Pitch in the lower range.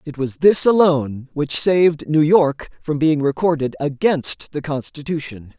No: medium, 150 Hz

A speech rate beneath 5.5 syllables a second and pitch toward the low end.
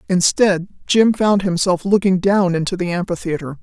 No: 4.9 syllables/s; medium, 185 Hz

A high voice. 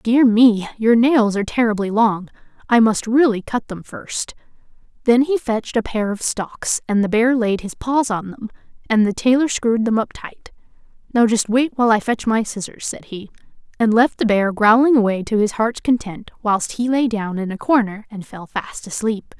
Yes: high, 225 Hz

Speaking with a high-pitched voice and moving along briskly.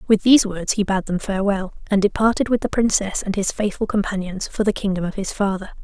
Yes: high, 200 Hz; fast, 225 wpm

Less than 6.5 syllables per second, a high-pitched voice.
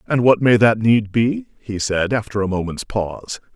No: 4.8 syllables/s; low, 110 Hz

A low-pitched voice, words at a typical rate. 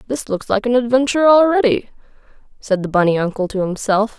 No: high, 225 Hz; average, 170 wpm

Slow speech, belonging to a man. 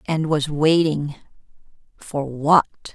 No: slow, 80 wpm; female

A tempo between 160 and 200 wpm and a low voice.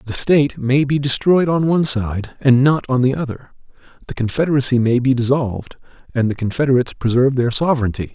Yes: average, 175 wpm; low, 130 Hz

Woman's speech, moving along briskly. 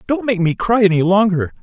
No: male; fast, 220 wpm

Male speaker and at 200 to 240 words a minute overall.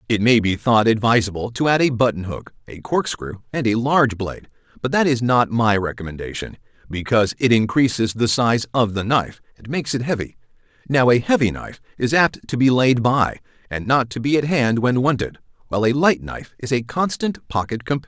Yes: male; fast, 205 wpm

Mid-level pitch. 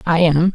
Yes: medium, 165 Hz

